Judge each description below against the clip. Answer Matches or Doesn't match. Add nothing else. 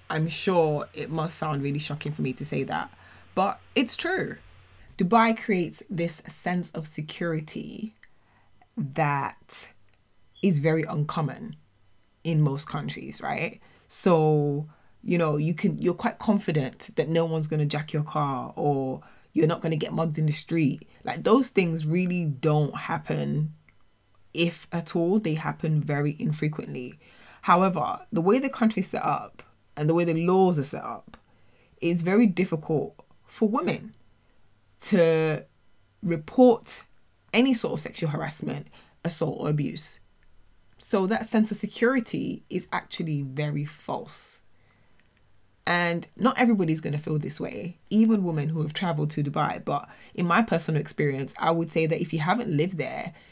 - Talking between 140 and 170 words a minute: Matches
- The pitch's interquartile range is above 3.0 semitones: Matches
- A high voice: Doesn't match